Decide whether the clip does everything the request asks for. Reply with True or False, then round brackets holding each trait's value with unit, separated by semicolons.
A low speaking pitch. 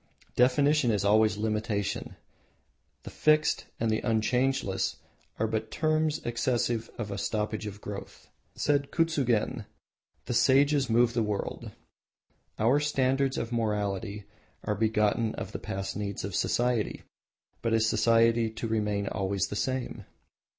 True (115 Hz)